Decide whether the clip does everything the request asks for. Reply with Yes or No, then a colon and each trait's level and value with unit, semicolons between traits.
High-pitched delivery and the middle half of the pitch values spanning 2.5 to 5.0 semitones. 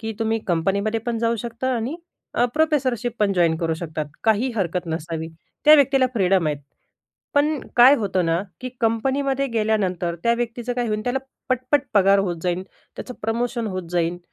No: high, 220 Hz; wide, 5.4 semitones